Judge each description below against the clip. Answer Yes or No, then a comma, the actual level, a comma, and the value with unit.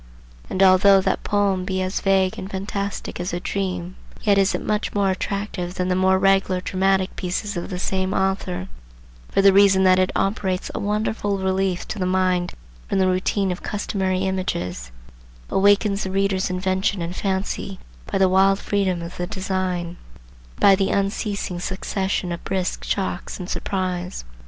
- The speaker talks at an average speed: Yes, average, 165 wpm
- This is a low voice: No, high, 190 Hz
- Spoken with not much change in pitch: Yes, narrow, 1.2 semitones